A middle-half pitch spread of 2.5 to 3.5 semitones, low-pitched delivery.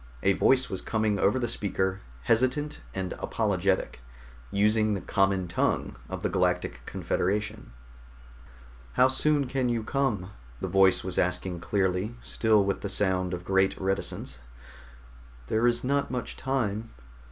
No: average, 4.0 semitones; low, 100 Hz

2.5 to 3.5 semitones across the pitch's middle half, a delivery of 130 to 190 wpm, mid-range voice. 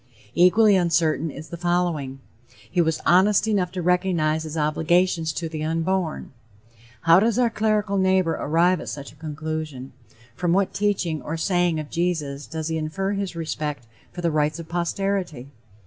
Yes: average, 3.1 semitones; average, 165 wpm; medium, 170 Hz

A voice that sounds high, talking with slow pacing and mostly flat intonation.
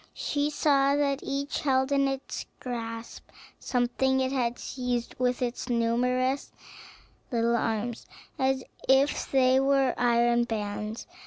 Yes: very high, 255 Hz; slow, 125 wpm; narrow, 2.3 semitones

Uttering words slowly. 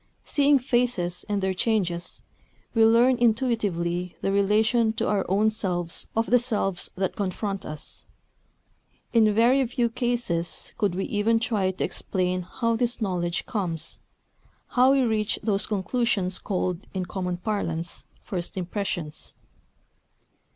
Yes: slow, 130 wpm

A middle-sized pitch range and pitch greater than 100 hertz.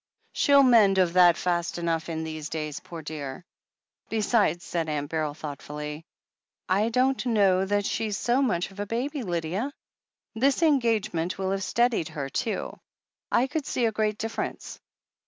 No: wide, 6.0 semitones; high, 190 Hz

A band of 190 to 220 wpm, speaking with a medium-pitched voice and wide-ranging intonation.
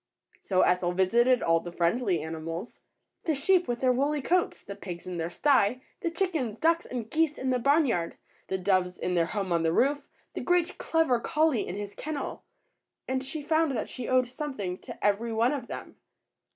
No: average, 200 wpm; high, 240 Hz; wide, 8.1 semitones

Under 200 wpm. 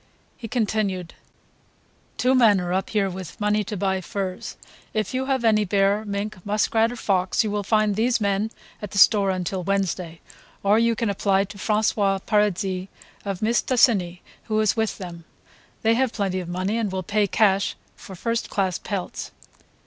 Yes: average, 170 wpm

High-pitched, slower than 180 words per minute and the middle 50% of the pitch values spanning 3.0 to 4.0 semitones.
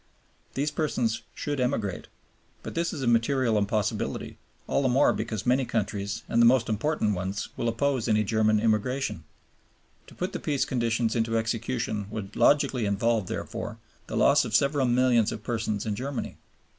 No: low, 115 Hz; average, 165 wpm; average, 3.4 semitones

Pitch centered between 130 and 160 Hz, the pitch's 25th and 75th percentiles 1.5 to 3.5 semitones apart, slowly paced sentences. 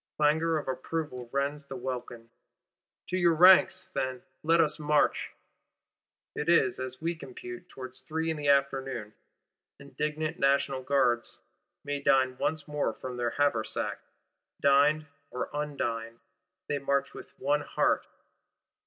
Yes: medium, 140 Hz; average, 2.9 semitones; slow, 130 wpm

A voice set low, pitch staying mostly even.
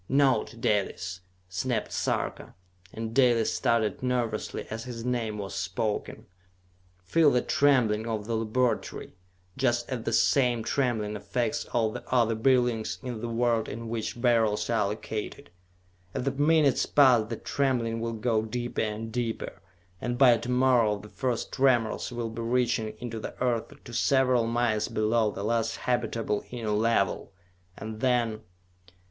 Yes: low, 115 Hz; narrow, 2.2 semitones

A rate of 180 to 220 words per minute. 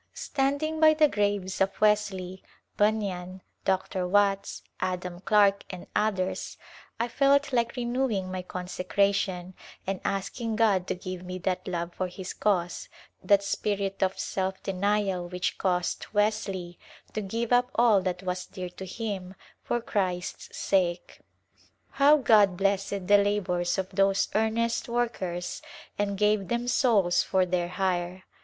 No: average, 140 wpm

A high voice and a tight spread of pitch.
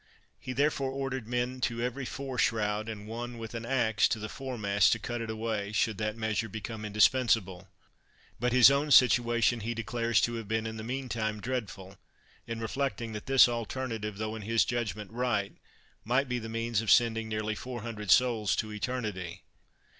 No: low, 115 Hz; narrow, 2.3 semitones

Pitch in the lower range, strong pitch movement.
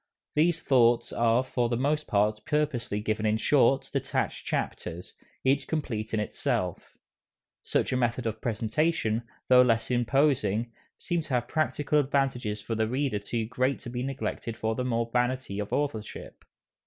No: low, 120 Hz; average, 3.6 semitones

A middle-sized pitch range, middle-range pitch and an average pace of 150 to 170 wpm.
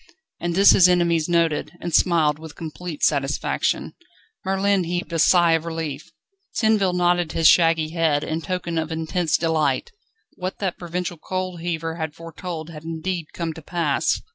No: narrow, 1.9 semitones; medium, 165 Hz; average, 160 wpm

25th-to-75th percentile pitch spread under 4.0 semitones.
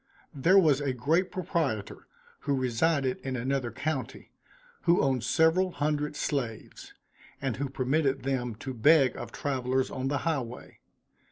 Yes: average, 3.3 semitones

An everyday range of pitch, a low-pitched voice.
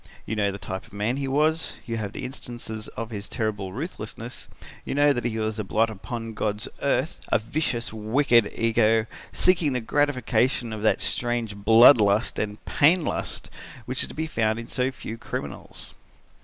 Yes: average, 3.1 semitones; low, 115 Hz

